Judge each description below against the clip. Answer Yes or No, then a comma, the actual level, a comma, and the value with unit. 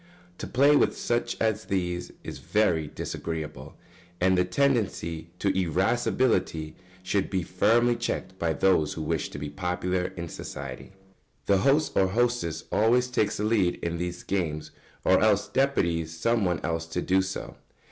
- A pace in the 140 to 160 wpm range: Yes, average, 155 wpm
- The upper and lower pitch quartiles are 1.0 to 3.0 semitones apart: No, average, 4.9 semitones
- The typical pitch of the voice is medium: No, very low, 95 Hz